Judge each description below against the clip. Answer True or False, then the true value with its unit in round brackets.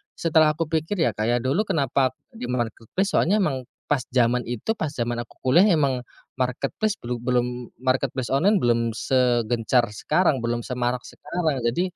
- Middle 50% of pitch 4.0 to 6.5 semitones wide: True (4.3 semitones)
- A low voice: True (125 Hz)